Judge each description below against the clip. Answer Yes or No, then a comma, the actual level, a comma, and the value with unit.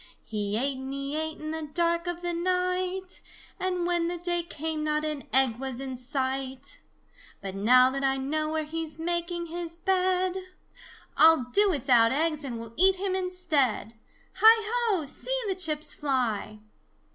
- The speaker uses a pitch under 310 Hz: No, very high, 315 Hz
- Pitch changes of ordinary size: Yes, average, 4.8 semitones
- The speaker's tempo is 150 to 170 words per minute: Yes, average, 165 wpm